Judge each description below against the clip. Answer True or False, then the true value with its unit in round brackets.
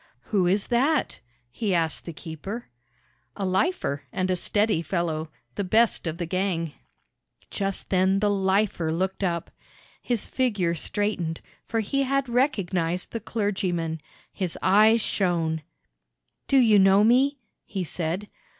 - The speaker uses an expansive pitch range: False (4.1 semitones)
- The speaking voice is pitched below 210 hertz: True (190 Hz)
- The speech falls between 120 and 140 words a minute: True (135 wpm)